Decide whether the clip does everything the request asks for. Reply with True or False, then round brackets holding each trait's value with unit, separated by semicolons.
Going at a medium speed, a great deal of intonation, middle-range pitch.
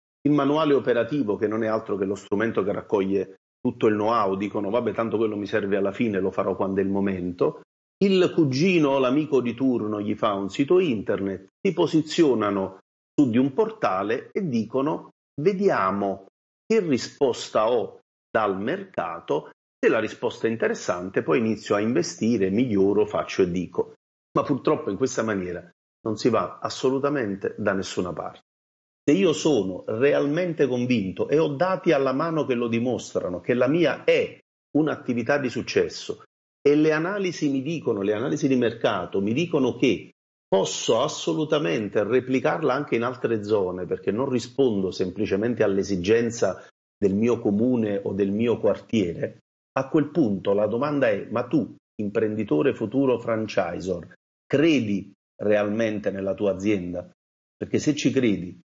False (155 wpm; 6.9 semitones; 115 Hz)